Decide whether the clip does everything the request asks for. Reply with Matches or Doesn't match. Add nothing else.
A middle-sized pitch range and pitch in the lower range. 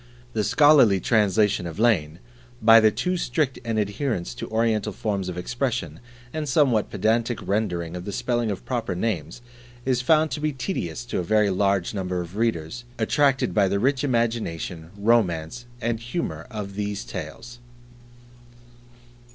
Matches